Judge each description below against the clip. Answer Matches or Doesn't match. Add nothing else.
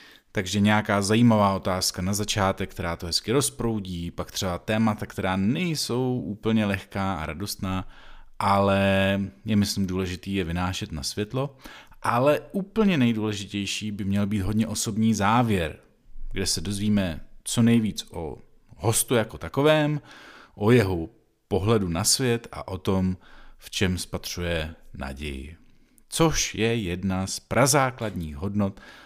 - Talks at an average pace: Matches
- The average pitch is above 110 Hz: Doesn't match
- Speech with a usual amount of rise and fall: Matches